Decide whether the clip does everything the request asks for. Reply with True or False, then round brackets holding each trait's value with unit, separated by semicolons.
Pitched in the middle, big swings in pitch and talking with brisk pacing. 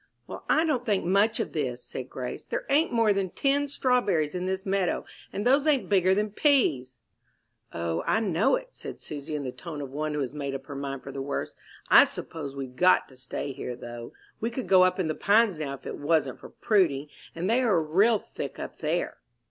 True (175 Hz; 7.8 semitones; 220 wpm)